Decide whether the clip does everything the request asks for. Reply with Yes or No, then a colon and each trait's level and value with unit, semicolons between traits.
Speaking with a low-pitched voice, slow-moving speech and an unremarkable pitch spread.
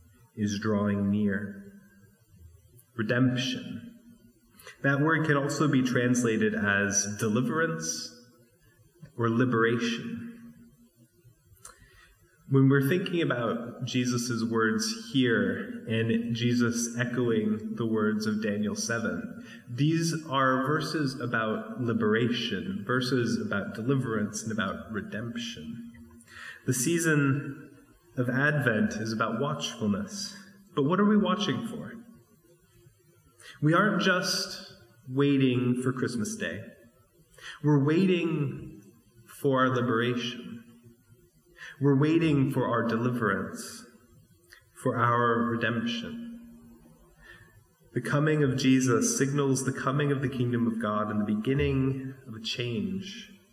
Yes: low, 125 Hz; slow, 100 wpm; average, 5.0 semitones